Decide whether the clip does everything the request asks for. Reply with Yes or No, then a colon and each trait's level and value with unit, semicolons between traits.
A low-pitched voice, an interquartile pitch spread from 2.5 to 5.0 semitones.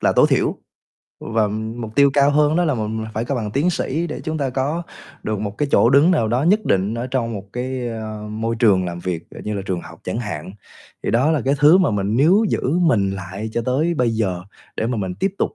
No: low, 120 Hz; wide, 5.5 semitones